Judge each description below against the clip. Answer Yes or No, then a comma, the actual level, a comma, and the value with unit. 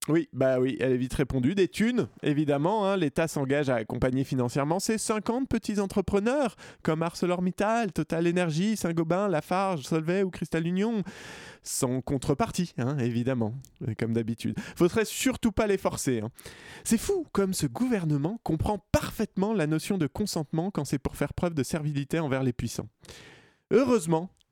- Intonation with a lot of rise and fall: Yes, wide, 6.3 semitones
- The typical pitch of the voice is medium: Yes, medium, 170 Hz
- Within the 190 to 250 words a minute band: No, average, 155 wpm